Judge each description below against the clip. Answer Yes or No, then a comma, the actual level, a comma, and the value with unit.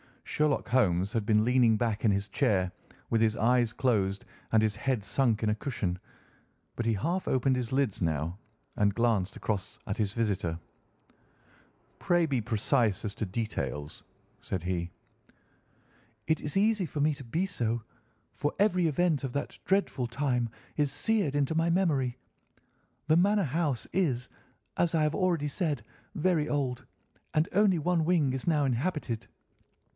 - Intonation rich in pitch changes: Yes, wide, 6.4 semitones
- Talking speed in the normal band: Yes, average, 160 wpm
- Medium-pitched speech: No, low, 130 Hz